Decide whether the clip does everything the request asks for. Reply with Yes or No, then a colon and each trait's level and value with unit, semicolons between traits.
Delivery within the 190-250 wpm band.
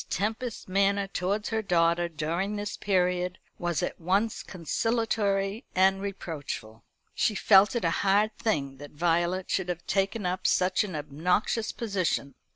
No: average, 145 wpm